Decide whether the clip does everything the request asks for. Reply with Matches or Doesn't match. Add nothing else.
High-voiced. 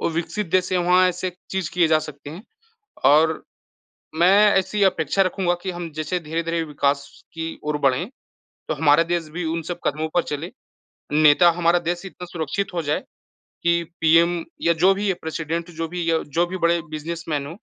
Doesn't match